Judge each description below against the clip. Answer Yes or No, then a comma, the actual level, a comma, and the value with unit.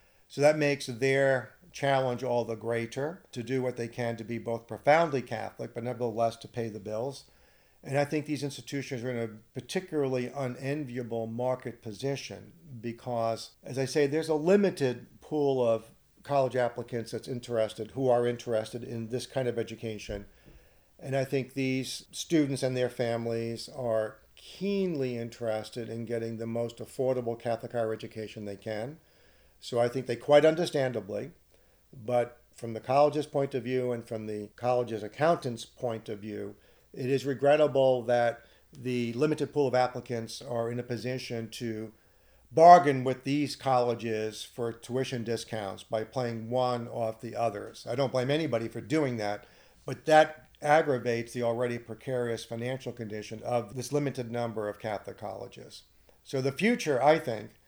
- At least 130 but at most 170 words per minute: Yes, average, 160 wpm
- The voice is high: No, low, 120 Hz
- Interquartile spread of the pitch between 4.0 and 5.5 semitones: No, average, 2.9 semitones